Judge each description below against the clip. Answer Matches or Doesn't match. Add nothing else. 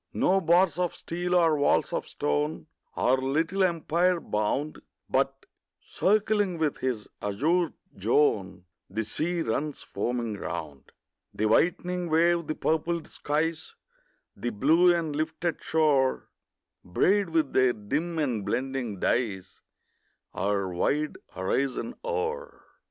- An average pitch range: Doesn't match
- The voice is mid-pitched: Matches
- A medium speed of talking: Doesn't match